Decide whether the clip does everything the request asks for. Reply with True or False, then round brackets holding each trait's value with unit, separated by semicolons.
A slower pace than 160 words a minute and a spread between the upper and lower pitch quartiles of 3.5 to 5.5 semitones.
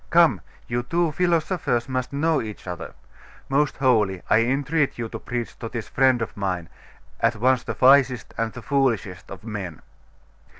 False (165 wpm; 4.0 semitones)